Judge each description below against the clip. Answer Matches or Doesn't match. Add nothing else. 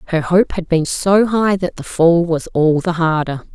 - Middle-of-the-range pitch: Matches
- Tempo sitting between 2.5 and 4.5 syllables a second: Matches